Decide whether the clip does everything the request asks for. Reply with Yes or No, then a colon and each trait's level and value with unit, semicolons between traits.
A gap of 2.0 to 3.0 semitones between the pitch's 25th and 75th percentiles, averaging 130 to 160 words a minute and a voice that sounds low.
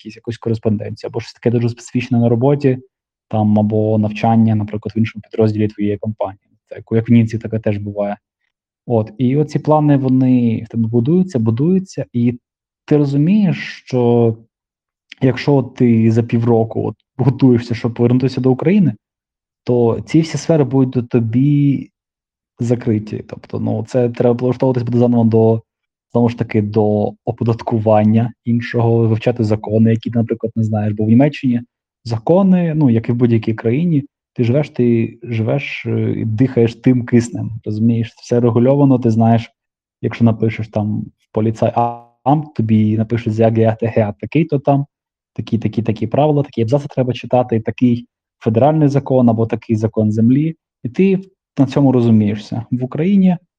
Yes: narrow, 2.6 semitones; average, 150 wpm; low, 120 Hz